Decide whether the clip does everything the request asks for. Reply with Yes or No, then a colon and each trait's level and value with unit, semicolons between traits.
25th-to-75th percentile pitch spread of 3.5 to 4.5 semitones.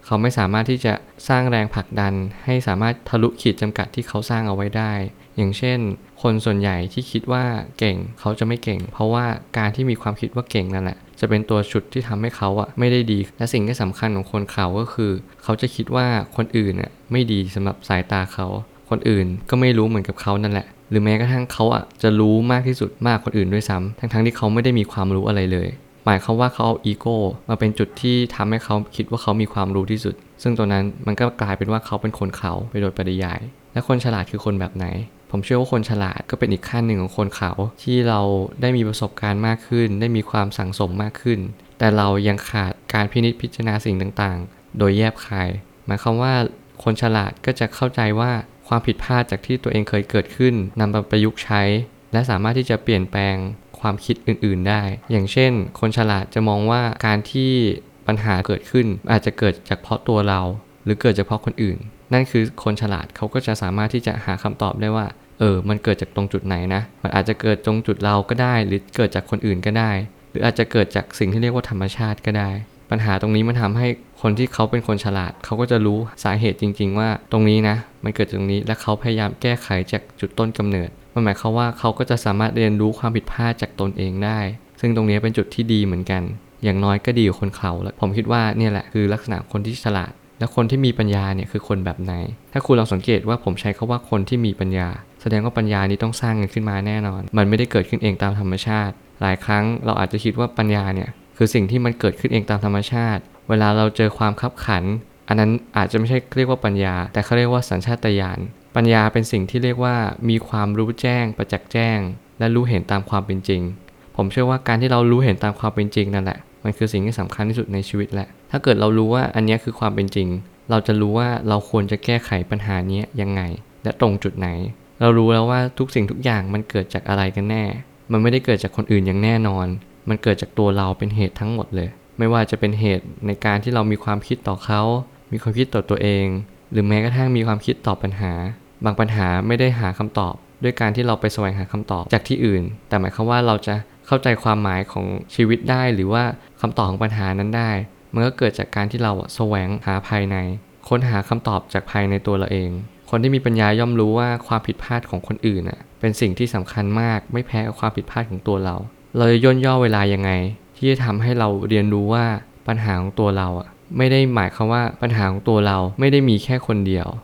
No: average, 2.8 semitones